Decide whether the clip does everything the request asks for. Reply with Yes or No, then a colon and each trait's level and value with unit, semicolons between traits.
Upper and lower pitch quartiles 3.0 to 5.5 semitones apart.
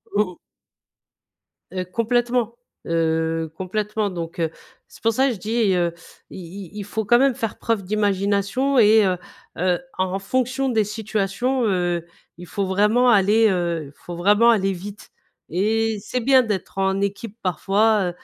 Yes: average, 3.5 semitones